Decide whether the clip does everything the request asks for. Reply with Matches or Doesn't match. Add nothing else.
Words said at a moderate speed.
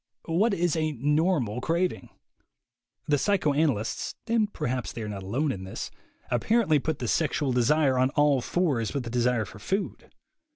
Matches